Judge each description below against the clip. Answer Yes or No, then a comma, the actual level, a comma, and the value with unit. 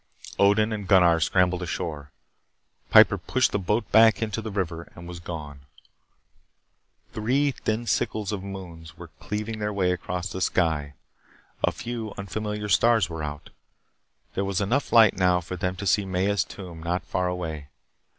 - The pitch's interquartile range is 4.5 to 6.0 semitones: No, average, 3.5 semitones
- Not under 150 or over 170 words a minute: Yes, average, 160 wpm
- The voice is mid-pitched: No, very low, 95 Hz